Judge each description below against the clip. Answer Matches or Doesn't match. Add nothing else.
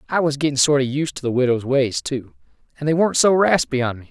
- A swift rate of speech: Matches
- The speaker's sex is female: Doesn't match